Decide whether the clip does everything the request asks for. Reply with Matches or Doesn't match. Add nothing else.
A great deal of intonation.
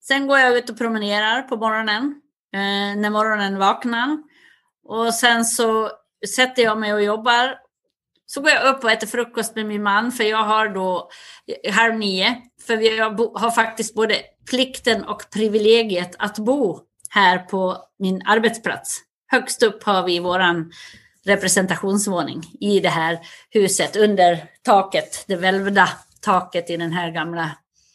Doesn't match